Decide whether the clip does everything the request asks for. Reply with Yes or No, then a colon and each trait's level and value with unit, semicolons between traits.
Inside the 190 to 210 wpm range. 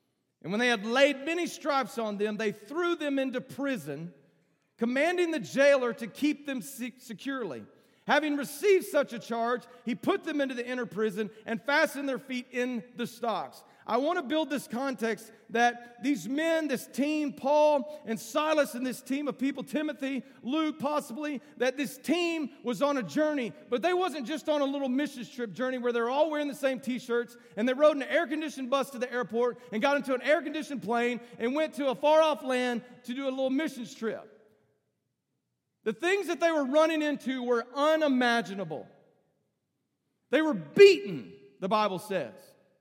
No: average, 180 wpm